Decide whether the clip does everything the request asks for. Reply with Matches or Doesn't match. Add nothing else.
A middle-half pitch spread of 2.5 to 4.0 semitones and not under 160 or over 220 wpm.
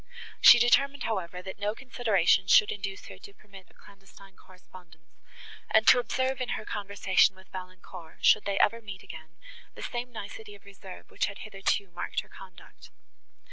Matches